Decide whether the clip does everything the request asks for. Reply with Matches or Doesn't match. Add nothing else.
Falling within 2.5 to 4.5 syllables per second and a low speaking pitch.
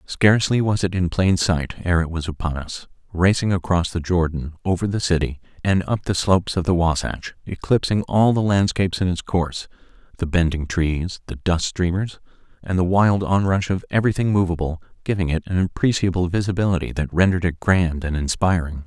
Doesn't match